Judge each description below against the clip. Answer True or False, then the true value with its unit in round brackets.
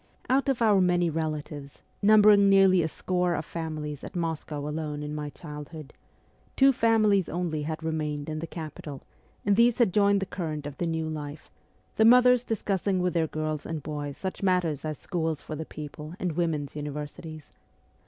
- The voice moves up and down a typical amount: True (4.2 semitones)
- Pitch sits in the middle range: True (160 Hz)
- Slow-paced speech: False (175 wpm)